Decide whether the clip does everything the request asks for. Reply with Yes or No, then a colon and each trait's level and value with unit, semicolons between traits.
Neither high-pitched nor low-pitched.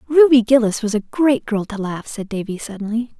No: high, 225 Hz